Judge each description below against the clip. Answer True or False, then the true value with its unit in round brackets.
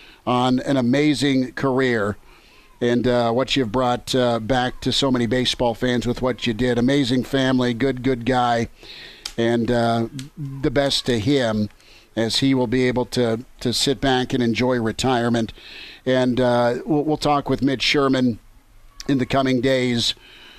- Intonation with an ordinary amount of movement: False (1.9 semitones)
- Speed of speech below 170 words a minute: True (150 wpm)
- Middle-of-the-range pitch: False (125 Hz)